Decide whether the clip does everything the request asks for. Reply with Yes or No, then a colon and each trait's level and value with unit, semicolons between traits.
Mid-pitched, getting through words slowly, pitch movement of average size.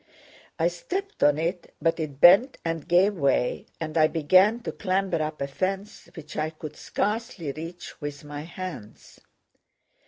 No: medium, 165 Hz; average, 155 wpm; average, 3.8 semitones